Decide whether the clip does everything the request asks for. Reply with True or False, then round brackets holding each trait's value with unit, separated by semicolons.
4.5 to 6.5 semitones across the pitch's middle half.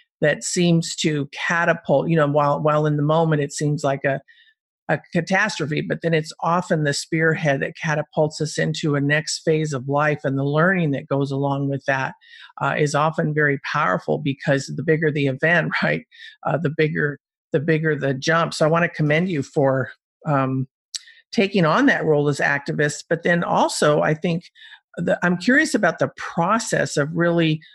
False (2.8 semitones)